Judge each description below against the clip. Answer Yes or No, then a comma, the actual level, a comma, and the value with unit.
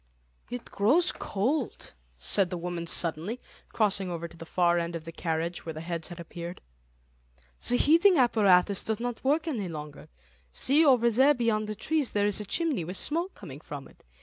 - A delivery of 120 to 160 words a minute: No, average, 185 wpm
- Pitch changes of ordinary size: No, wide, 6.5 semitones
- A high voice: Yes, high, 200 Hz